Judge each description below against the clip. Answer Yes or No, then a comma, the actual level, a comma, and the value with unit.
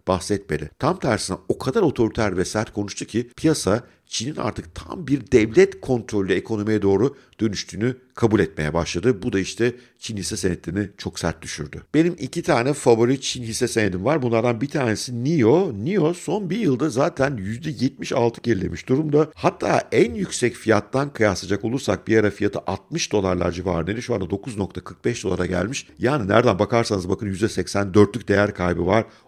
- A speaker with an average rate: No, fast, 160 wpm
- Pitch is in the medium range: No, low, 110 Hz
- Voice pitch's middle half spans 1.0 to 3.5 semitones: No, average, 4.7 semitones